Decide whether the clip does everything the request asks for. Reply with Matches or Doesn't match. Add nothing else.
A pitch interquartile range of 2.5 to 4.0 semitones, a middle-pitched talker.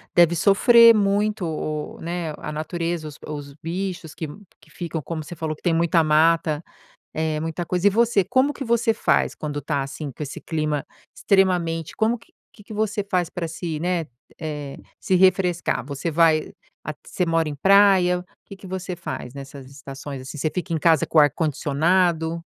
Matches